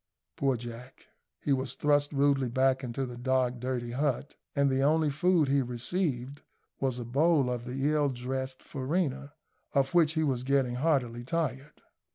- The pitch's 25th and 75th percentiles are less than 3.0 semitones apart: Yes, narrow, 2.6 semitones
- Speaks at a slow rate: No, average, 165 wpm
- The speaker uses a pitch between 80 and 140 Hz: Yes, low, 135 Hz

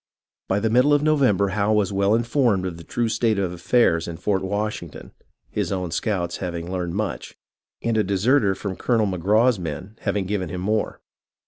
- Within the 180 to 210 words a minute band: Yes, average, 185 wpm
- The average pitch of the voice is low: Yes, low, 100 Hz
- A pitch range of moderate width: Yes, average, 3.5 semitones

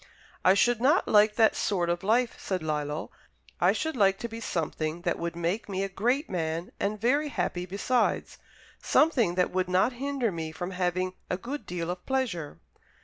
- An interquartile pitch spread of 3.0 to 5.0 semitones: No, wide, 5.4 semitones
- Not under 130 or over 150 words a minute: No, average, 185 wpm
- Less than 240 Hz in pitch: Yes, high, 190 Hz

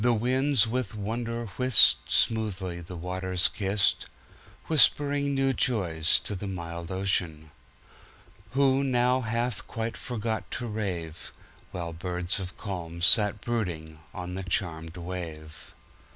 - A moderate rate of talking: No, slow, 110 wpm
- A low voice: Yes, very low, 95 Hz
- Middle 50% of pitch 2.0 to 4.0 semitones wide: No, wide, 5.4 semitones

